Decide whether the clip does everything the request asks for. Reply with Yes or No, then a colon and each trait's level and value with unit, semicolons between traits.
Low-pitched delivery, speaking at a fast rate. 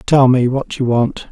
Yes: low, 130 Hz; fast, 230 wpm